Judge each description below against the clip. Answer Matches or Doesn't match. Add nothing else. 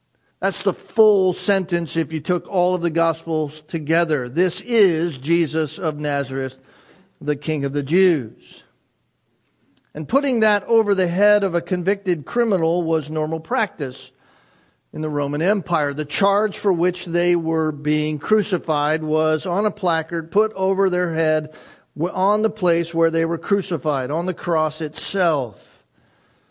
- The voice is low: Doesn't match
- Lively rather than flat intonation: Doesn't match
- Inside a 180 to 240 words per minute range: Doesn't match